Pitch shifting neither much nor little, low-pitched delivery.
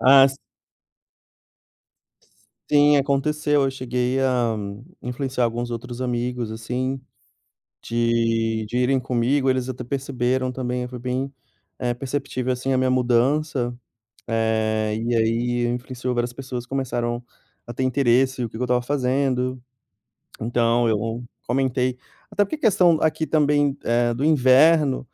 No: narrow, 2.0 semitones; low, 125 Hz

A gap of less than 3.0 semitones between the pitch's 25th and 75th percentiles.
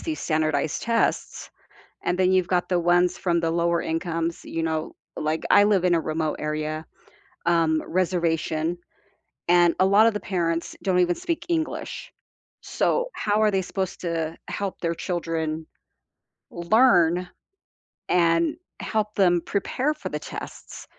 Yes: narrow, 2.6 semitones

